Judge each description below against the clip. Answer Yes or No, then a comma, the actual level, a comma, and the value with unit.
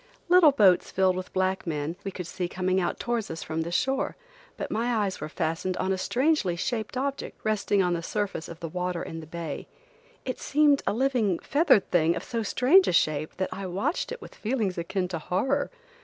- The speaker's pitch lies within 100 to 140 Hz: No, high, 190 Hz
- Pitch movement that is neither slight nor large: No, wide, 6.0 semitones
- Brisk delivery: Yes, fast, 210 wpm